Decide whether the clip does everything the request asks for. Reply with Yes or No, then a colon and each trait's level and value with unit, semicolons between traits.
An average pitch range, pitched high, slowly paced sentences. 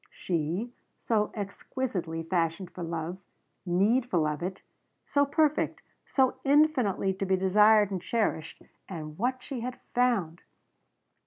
No: wide, 6.2 semitones; high, 195 Hz; slow, 120 wpm